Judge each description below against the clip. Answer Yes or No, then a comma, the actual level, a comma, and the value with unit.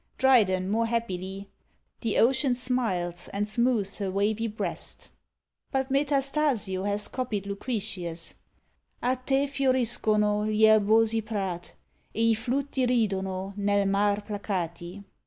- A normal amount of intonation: Yes, average, 3.8 semitones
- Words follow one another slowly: Yes, slow, 115 wpm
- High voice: Yes, high, 215 Hz